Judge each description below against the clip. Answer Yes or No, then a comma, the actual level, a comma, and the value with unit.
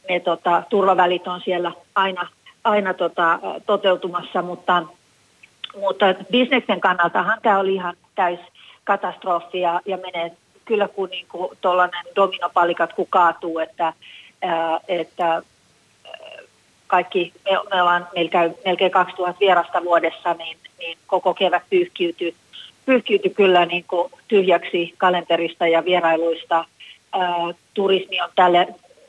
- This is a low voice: No, medium, 180 Hz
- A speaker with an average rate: Yes, average, 115 wpm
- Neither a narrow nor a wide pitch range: No, narrow, 1.8 semitones